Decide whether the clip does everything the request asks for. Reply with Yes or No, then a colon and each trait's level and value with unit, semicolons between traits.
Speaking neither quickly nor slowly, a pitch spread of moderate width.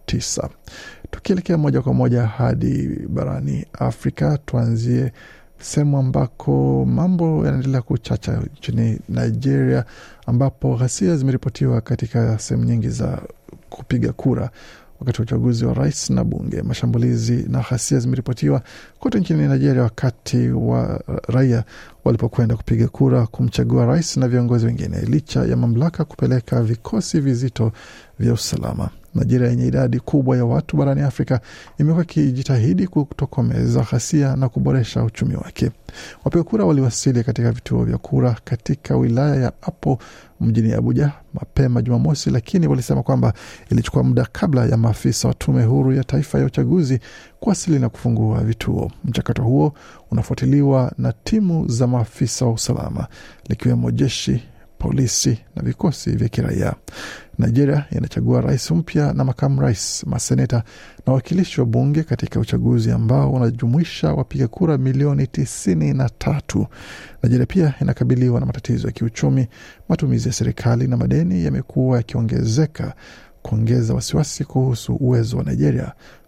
Yes: average, 130 wpm; average, 3.5 semitones